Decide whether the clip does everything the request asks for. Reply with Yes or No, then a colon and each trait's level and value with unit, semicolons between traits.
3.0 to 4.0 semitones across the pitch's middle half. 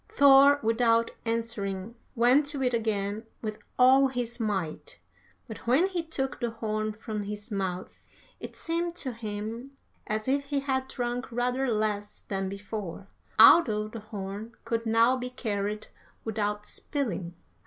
Yes: average, 3.7 semitones